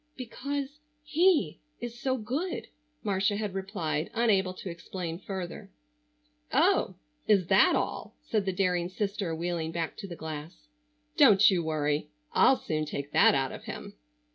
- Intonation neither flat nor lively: Yes, average, 4.9 semitones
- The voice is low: No, high, 190 Hz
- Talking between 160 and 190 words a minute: No, average, 145 wpm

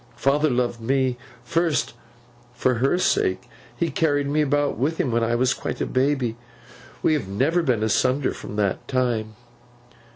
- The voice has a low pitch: Yes, low, 130 Hz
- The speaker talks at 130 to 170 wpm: Yes, average, 160 wpm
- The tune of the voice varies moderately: Yes, average, 3.6 semitones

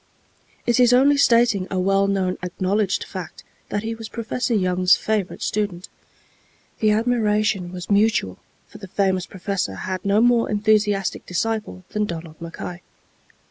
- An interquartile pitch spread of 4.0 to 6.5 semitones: No, average, 3.0 semitones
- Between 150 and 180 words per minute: No, average, 140 wpm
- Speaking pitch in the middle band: No, high, 200 Hz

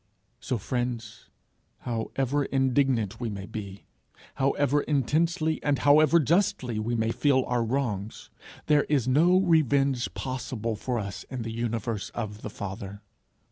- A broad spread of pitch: No, average, 4.3 semitones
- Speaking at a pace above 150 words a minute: No, average, 140 wpm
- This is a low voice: Yes, low, 125 Hz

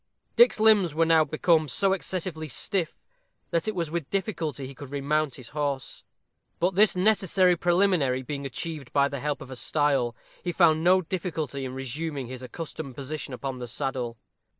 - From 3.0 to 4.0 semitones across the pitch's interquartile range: No, average, 4.5 semitones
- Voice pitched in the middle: Yes, medium, 155 Hz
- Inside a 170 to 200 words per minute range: Yes, average, 175 wpm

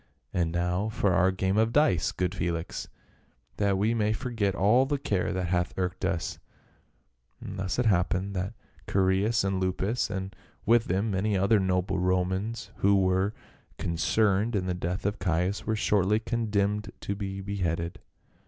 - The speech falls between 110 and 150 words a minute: No, average, 160 wpm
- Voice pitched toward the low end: Yes, very low, 95 Hz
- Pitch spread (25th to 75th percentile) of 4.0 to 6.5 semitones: No, narrow, 2.4 semitones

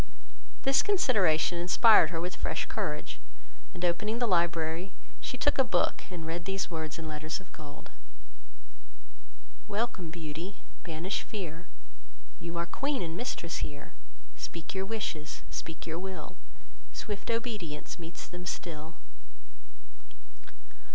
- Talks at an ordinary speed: No, slow, 125 wpm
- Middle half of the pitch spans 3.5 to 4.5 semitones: Yes, average, 3.9 semitones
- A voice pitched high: No, medium, 175 Hz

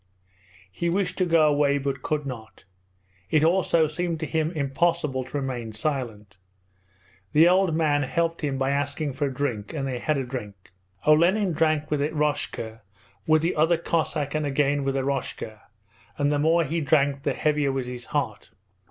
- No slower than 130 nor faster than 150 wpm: No, average, 170 wpm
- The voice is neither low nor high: Yes, medium, 145 Hz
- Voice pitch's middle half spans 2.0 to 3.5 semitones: Yes, average, 2.9 semitones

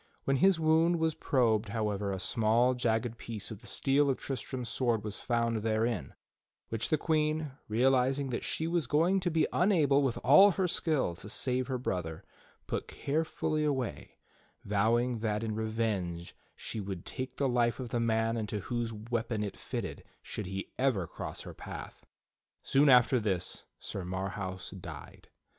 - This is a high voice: No, low, 120 Hz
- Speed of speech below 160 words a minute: No, average, 165 wpm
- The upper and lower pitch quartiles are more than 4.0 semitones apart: Yes, average, 4.4 semitones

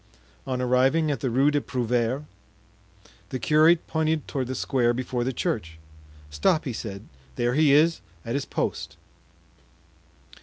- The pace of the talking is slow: No, average, 145 wpm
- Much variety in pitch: No, average, 3.8 semitones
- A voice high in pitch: No, low, 130 Hz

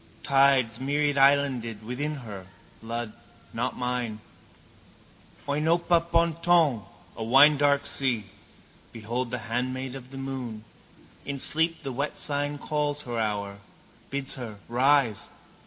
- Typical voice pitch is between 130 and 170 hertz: Yes, low, 135 Hz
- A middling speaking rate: No, slow, 110 wpm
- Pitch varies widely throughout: No, average, 3.7 semitones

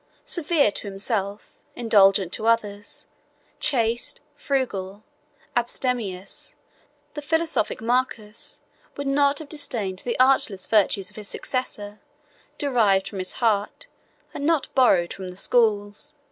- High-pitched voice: Yes, high, 225 Hz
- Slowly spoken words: Yes, slow, 120 wpm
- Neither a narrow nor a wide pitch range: Yes, average, 4.8 semitones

